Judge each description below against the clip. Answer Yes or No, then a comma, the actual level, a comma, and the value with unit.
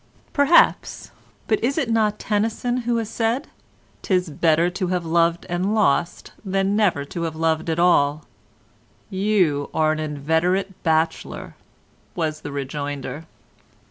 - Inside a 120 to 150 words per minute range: Yes, slow, 135 wpm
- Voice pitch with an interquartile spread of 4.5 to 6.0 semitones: Yes, average, 5.1 semitones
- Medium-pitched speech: Yes, medium, 175 Hz